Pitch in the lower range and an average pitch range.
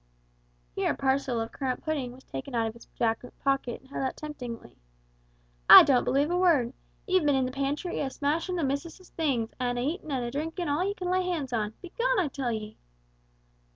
No: very high, 275 Hz; average, 4.8 semitones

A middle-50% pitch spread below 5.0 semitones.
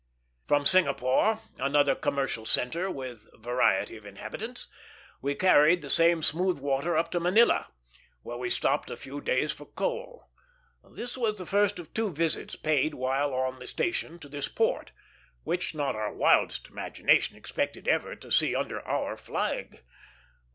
No: wide, 5.4 semitones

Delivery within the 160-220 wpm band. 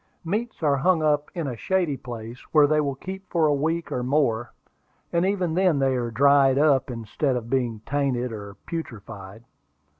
Yes: average, 180 wpm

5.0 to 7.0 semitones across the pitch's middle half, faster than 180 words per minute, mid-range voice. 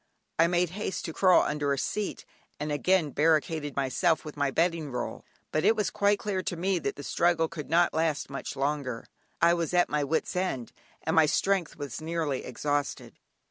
No: average, 3.3 semitones; average, 190 wpm; medium, 160 Hz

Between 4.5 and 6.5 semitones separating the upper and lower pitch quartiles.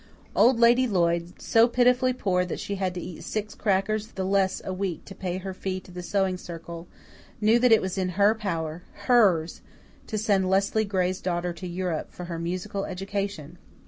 No: average, 2.8 semitones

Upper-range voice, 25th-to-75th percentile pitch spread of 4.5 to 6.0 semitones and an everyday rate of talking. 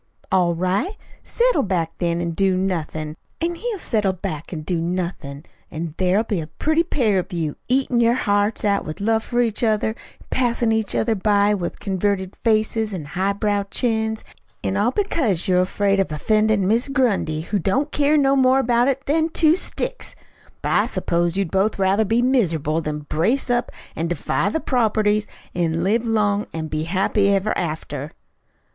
Yes: high, 205 Hz; average, 5.2 semitones; average, 175 wpm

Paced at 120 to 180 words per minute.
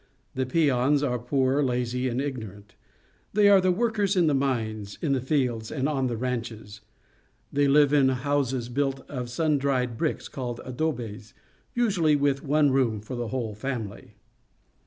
Yes: average, 160 wpm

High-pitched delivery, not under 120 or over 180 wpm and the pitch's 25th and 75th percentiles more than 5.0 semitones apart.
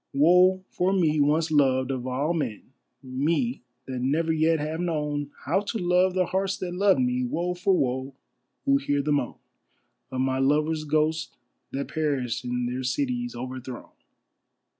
No: medium, 150 Hz; average, 160 wpm; wide, 5.4 semitones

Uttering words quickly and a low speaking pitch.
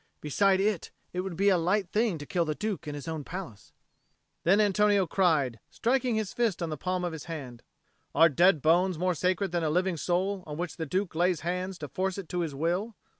No: fast, 225 wpm; medium, 180 Hz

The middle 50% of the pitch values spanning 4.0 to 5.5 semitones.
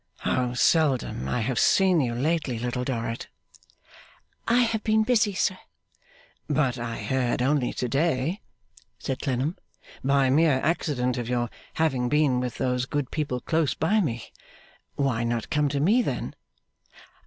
Yes: average, 4.5 semitones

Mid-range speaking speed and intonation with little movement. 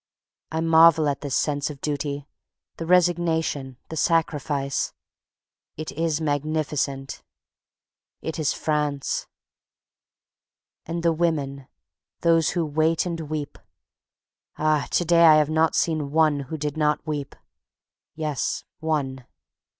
No: slow, 120 wpm; narrow, 2.1 semitones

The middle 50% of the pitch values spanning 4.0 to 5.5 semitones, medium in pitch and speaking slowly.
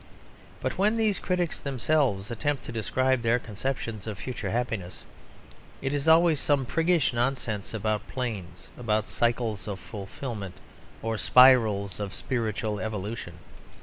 No: average, 4.4 semitones; low, 115 Hz; slow, 130 wpm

